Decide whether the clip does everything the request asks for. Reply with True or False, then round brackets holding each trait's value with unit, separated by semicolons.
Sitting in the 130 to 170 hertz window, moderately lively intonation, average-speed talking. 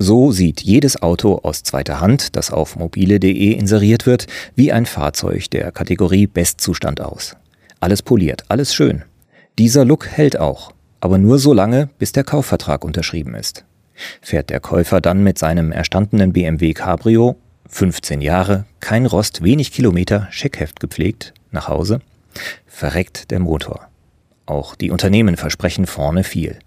False (95 Hz; 4.7 semitones; 145 wpm)